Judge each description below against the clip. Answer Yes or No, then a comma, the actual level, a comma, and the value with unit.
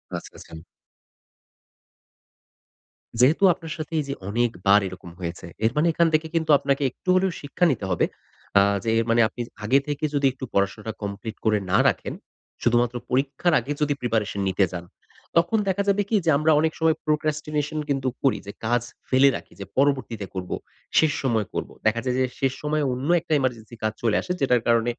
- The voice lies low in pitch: Yes, low, 130 Hz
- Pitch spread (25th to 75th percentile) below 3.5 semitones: No, wide, 5.4 semitones